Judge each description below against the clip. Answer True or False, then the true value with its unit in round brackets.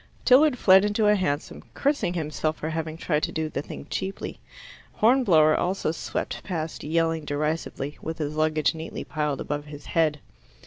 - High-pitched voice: False (160 Hz)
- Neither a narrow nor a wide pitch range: True (3.6 semitones)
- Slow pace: False (165 wpm)